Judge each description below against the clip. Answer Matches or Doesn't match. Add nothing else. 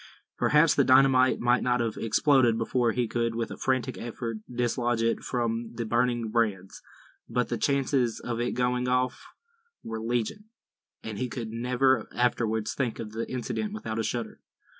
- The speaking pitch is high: Doesn't match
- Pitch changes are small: Matches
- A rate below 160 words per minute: Doesn't match